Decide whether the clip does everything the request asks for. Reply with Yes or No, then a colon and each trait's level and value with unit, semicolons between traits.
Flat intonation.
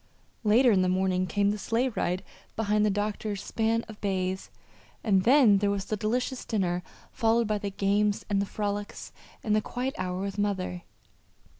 Yes: narrow, 2.3 semitones